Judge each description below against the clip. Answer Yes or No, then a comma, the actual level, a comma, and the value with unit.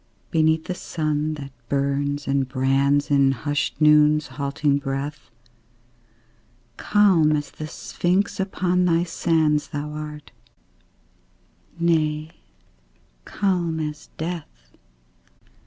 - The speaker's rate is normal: No, slow, 95 wpm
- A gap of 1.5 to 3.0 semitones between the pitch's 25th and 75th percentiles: Yes, narrow, 2.4 semitones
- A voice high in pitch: No, medium, 150 Hz